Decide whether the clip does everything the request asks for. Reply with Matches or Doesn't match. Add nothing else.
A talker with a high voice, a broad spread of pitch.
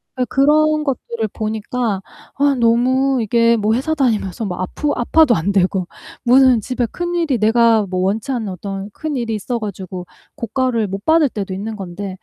Doesn't match